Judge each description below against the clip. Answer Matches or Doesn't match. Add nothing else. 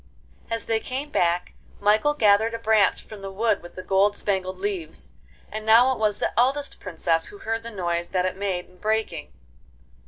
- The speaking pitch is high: Matches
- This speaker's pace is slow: Doesn't match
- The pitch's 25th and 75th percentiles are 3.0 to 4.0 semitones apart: Matches